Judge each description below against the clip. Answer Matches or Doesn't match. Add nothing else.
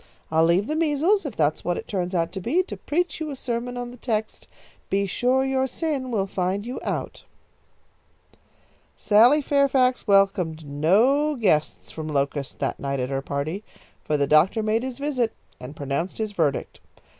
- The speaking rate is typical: Matches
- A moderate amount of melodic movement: Doesn't match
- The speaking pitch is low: Doesn't match